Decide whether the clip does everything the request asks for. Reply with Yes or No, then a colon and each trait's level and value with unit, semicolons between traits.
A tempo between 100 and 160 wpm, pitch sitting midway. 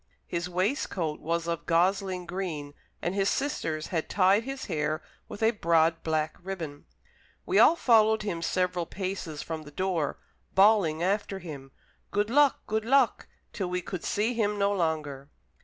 Yes: average, 155 wpm; medium, 180 Hz